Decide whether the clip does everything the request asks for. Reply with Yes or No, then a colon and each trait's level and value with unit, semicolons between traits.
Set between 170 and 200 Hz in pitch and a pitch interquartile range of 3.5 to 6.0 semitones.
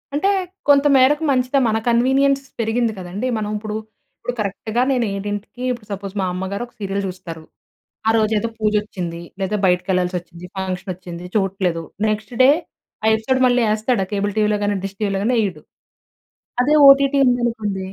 No: high, 210 Hz; average, 4.3 semitones